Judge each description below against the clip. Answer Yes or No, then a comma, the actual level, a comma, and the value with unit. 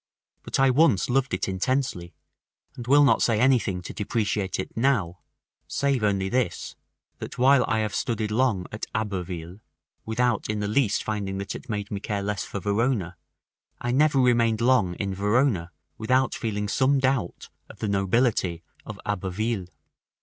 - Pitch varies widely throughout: No, average, 4.3 semitones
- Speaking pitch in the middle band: No, low, 110 Hz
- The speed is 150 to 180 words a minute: Yes, average, 160 wpm